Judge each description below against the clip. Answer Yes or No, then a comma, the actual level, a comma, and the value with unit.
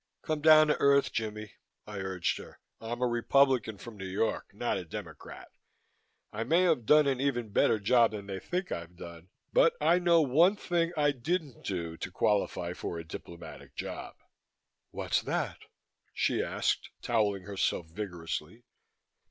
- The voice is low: Yes, low, 115 Hz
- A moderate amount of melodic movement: No, wide, 7.6 semitones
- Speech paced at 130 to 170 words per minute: Yes, average, 160 wpm